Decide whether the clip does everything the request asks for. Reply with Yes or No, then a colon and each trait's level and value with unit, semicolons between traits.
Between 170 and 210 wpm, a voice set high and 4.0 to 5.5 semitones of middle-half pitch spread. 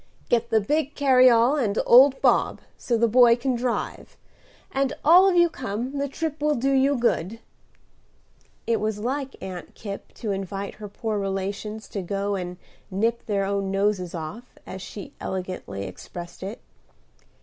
No: average, 160 wpm; high, 220 Hz; average, 4.8 semitones